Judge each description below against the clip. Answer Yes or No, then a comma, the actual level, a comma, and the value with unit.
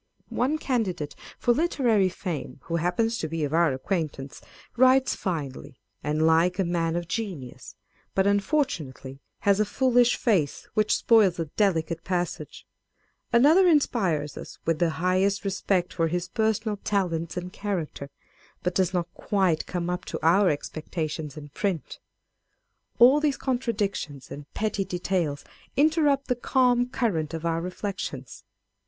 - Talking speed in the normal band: Yes, average, 145 wpm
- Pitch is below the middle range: No, medium, 185 Hz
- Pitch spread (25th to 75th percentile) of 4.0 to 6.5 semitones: Yes, wide, 5.6 semitones